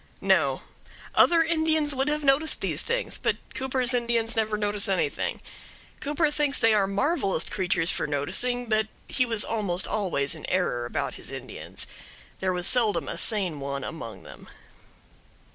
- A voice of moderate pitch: No, high, 220 Hz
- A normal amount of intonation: No, wide, 6.9 semitones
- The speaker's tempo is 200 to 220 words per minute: No, average, 155 wpm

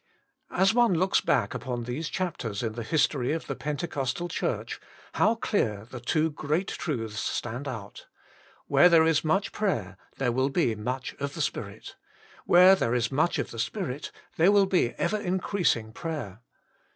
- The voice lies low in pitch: No, medium, 145 Hz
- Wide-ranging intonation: Yes, wide, 6.8 semitones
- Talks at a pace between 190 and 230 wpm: No, average, 165 wpm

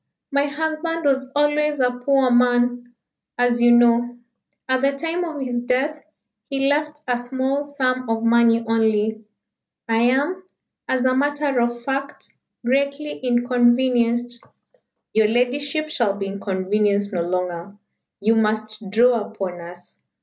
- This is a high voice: Yes, high, 245 Hz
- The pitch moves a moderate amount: Yes, average, 3.6 semitones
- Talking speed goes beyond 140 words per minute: No, slow, 135 wpm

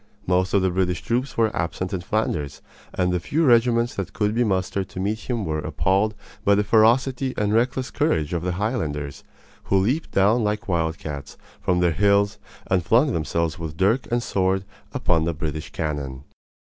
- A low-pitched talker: Yes, very low, 95 Hz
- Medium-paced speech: Yes, average, 180 wpm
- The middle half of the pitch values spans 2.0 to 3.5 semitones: No, average, 5.0 semitones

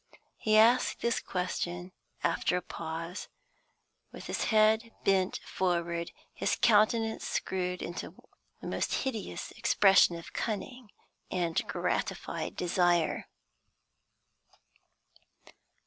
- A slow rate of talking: Yes, slow, 95 wpm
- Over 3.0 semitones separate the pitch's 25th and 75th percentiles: Yes, average, 4.0 semitones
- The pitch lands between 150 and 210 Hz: Yes, high, 190 Hz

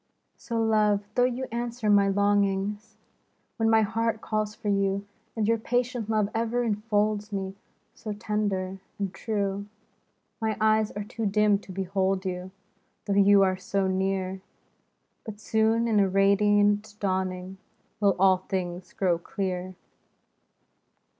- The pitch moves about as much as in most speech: No, narrow, 2.1 semitones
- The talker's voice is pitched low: No, high, 205 Hz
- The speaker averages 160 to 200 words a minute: No, average, 140 wpm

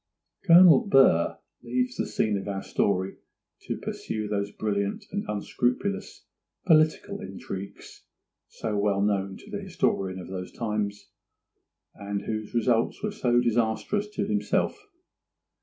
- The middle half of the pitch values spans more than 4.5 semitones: Yes, average, 5.0 semitones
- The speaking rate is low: Yes, slow, 125 wpm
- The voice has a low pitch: Yes, low, 110 Hz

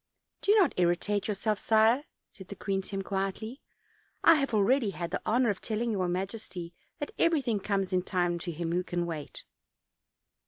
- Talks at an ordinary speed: Yes, average, 180 wpm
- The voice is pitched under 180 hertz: No, high, 200 Hz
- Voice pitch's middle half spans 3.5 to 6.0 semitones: Yes, average, 3.9 semitones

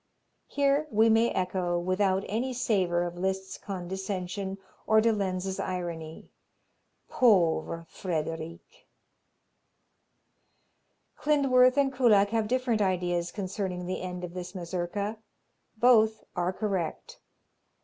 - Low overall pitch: No, high, 190 Hz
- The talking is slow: Yes, slow, 105 wpm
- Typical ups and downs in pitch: Yes, average, 3.7 semitones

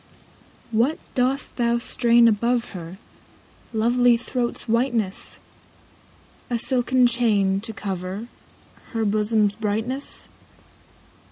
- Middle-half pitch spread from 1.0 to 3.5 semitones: Yes, average, 2.7 semitones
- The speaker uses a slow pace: Yes, slow, 90 wpm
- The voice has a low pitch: No, high, 230 Hz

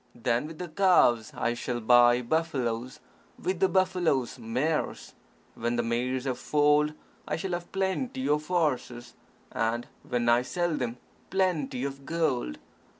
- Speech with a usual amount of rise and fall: No, wide, 5.8 semitones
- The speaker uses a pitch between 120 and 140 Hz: Yes, low, 135 Hz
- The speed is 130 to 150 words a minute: Yes, average, 145 wpm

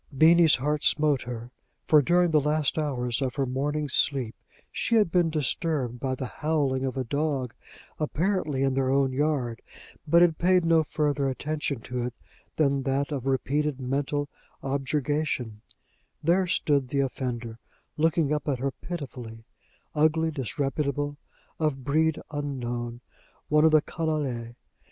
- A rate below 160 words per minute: Yes, average, 145 wpm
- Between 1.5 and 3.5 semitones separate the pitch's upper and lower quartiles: Yes, average, 3.0 semitones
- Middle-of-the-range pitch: Yes, medium, 145 Hz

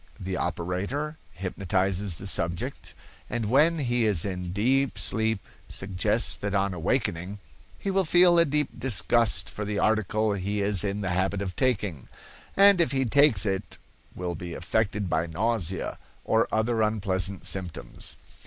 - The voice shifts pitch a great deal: No, average, 4.3 semitones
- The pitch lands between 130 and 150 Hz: No, low, 100 Hz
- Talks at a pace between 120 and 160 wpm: Yes, average, 150 wpm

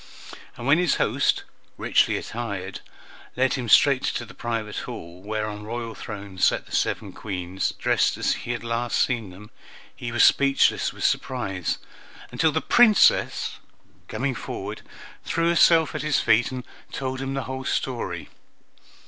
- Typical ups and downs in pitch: Yes, average, 4.1 semitones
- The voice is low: Yes, low, 120 Hz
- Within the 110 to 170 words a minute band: Yes, average, 155 wpm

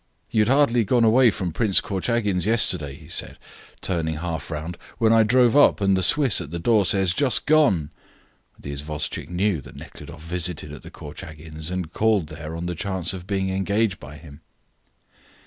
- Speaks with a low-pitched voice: Yes, very low, 95 Hz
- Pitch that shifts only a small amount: No, wide, 5.5 semitones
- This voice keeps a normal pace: Yes, average, 180 wpm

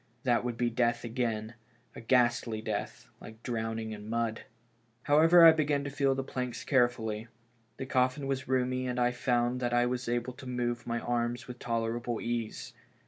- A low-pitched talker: Yes, low, 120 Hz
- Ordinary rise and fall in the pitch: No, narrow, 1.6 semitones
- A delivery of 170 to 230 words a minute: Yes, average, 175 wpm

